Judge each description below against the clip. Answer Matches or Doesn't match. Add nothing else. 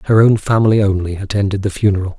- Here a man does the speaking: Matches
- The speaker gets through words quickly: Doesn't match